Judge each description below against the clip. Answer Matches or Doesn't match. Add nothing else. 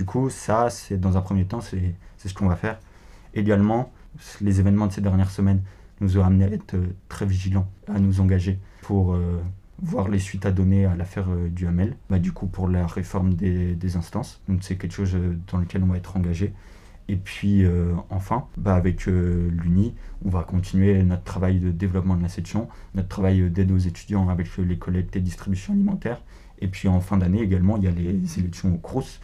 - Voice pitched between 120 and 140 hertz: Doesn't match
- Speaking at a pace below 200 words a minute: Doesn't match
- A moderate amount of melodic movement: Doesn't match